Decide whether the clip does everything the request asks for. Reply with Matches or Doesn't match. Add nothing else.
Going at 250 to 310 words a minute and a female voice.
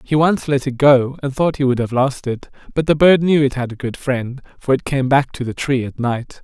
Doesn't match